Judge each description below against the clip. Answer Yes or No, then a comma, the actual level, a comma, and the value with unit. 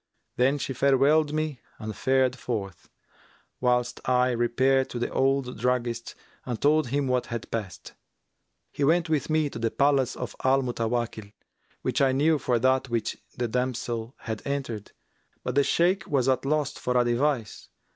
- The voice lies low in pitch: Yes, low, 130 Hz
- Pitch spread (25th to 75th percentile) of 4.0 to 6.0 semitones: No, average, 2.7 semitones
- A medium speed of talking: Yes, average, 165 wpm